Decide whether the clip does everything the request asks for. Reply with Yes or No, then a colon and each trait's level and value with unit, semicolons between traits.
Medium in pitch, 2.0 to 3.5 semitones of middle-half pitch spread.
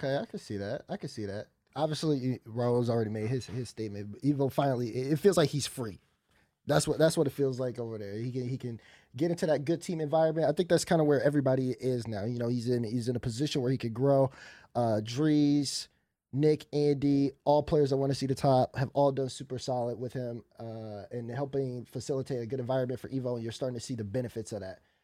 No: low, 130 Hz; average, 3.2 semitones